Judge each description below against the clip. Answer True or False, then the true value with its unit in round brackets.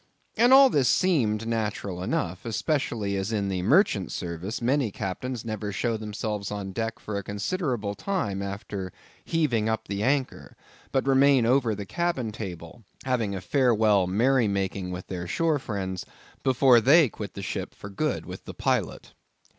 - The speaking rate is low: False (160 wpm)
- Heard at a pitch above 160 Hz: False (110 Hz)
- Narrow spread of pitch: False (4.9 semitones)